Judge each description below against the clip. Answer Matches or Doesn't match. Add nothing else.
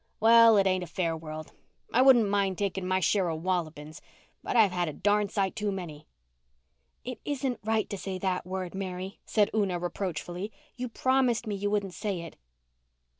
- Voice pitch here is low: Doesn't match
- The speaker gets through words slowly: Doesn't match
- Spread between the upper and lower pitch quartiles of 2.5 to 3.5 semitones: Matches